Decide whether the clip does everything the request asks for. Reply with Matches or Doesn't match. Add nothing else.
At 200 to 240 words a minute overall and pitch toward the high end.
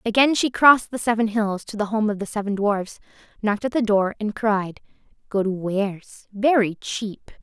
Doesn't match